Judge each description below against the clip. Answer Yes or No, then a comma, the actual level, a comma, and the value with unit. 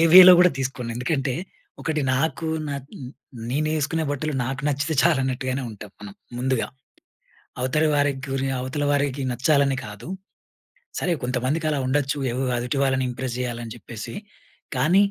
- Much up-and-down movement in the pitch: No, average, 2.9 semitones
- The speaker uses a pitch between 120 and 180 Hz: Yes, low, 135 Hz